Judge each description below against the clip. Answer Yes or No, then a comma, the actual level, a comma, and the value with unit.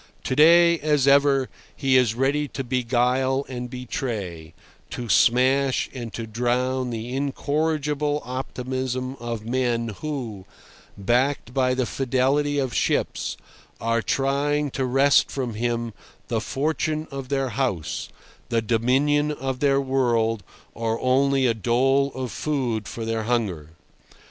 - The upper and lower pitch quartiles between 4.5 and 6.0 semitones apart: No, average, 2.8 semitones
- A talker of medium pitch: No, low, 130 Hz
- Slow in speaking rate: Yes, slow, 130 wpm